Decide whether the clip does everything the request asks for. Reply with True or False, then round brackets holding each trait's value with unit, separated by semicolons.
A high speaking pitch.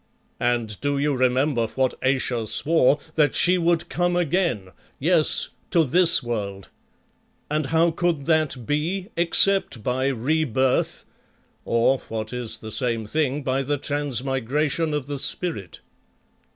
False (140 Hz)